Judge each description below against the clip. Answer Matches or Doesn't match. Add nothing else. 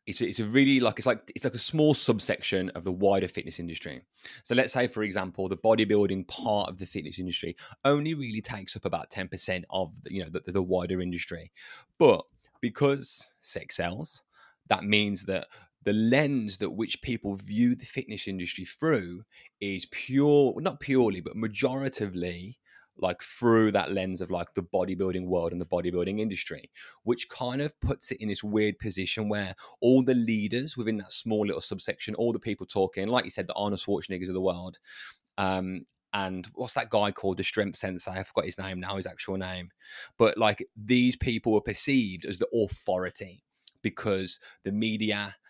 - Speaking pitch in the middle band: Doesn't match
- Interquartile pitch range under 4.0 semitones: Doesn't match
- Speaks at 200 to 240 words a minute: Doesn't match